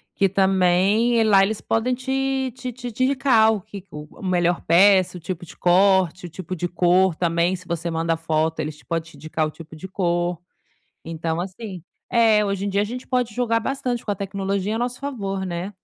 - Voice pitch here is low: No, high, 190 Hz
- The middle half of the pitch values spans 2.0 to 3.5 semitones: No, average, 4.5 semitones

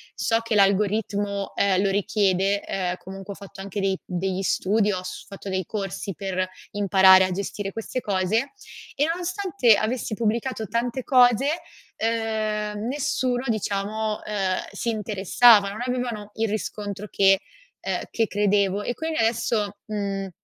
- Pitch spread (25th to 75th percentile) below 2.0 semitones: No, narrow, 2.6 semitones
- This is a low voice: No, high, 210 Hz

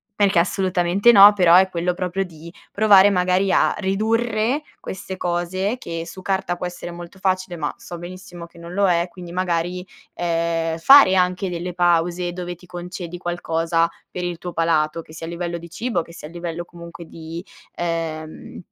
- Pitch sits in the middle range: Yes, medium, 175 Hz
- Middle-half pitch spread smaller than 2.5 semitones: Yes, narrow, 1.9 semitones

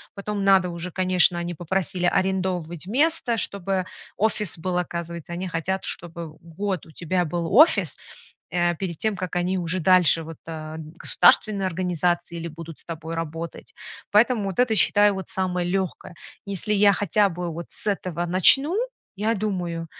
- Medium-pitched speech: Yes, medium, 180 Hz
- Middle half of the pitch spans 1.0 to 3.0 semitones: Yes, narrow, 2.6 semitones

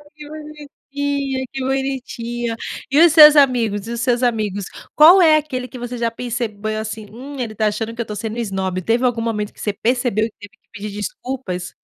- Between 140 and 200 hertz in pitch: No, high, 240 Hz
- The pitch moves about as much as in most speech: Yes, average, 3.8 semitones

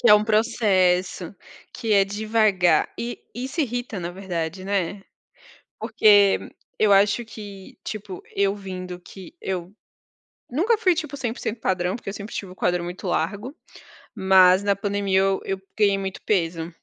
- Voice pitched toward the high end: Yes, high, 200 Hz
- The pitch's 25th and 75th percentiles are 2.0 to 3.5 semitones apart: Yes, average, 2.7 semitones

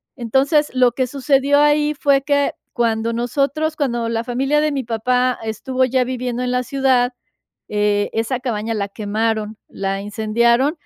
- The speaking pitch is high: Yes, very high, 250 Hz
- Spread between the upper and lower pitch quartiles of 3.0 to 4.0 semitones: Yes, average, 3.4 semitones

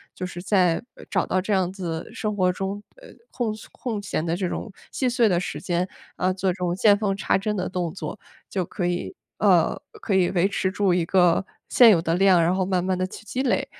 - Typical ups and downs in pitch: No, narrow, 2.3 semitones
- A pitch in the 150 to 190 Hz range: Yes, medium, 185 Hz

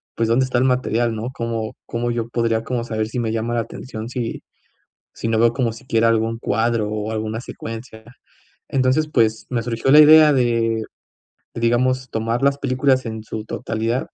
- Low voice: Yes, low, 115 Hz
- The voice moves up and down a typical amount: No, narrow, 2.2 semitones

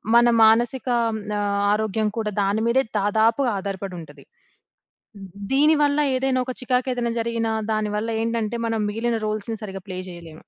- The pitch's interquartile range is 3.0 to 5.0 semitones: No, narrow, 2.4 semitones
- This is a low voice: No, high, 225 Hz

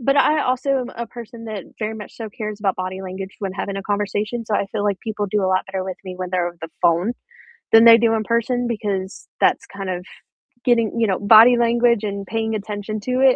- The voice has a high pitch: Yes, high, 210 Hz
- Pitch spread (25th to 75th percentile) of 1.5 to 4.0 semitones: Yes, average, 3.2 semitones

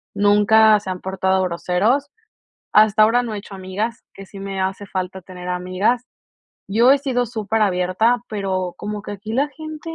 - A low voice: No, high, 205 Hz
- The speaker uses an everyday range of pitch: Yes, average, 3.2 semitones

